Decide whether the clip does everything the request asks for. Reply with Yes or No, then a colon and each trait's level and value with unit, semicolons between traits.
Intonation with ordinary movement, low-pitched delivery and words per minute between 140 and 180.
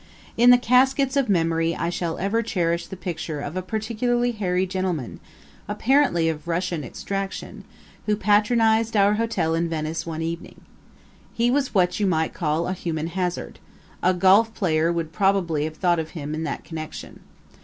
No: average, 4.8 semitones; medium, 180 Hz; average, 165 wpm